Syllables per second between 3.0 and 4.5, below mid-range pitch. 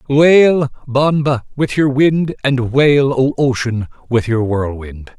Yes: 3.4 syllables/s; low, 130 Hz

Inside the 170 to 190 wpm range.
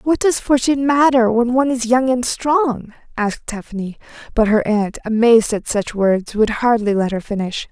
Yes: average, 185 wpm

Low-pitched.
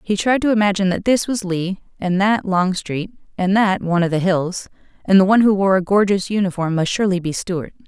No: high, 190 Hz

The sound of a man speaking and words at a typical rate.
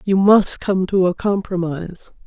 No: female; average, 160 wpm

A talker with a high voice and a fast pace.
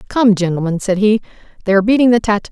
Yes: high, 210 Hz; fast, 215 wpm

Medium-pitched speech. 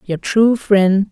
No: high, 205 Hz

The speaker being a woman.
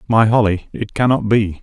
No: male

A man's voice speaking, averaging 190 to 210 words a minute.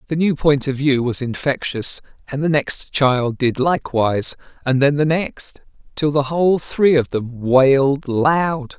No: male; average, 170 wpm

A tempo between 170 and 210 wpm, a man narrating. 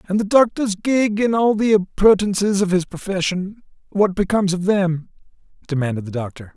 No: average, 155 wpm; male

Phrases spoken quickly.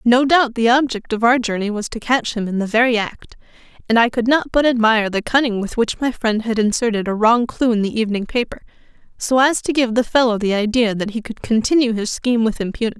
Yes: fast, 240 wpm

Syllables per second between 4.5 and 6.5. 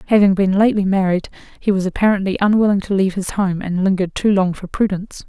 No: 6.8 syllables/s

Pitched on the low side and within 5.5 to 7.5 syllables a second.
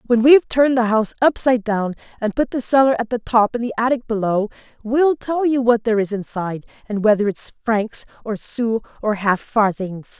No: high, 230 Hz; 5.6 syllables/s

